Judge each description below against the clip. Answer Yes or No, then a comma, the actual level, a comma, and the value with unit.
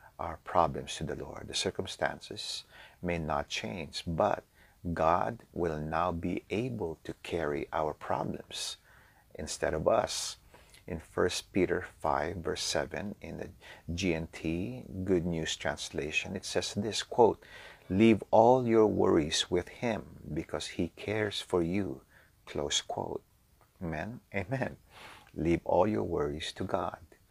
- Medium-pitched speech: No, very low, 90 Hz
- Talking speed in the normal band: No, slow, 130 wpm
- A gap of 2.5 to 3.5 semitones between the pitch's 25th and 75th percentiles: No, average, 4.1 semitones